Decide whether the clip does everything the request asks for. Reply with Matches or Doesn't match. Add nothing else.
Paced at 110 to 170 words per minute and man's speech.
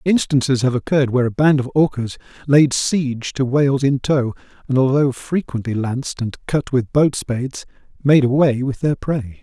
Doesn't match